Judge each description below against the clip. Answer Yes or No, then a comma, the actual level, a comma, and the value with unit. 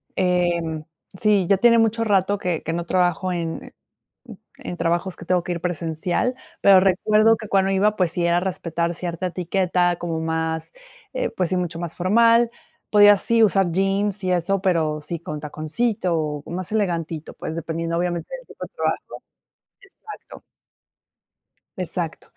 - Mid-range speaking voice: Yes, medium, 180 Hz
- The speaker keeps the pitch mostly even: No, average, 3.0 semitones